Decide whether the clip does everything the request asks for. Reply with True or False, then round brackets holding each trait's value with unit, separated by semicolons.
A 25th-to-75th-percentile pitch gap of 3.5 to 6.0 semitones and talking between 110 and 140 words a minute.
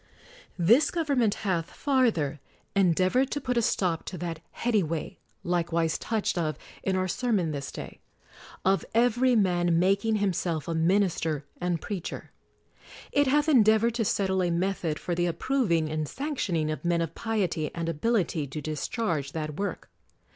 False (5.3 semitones; 155 wpm)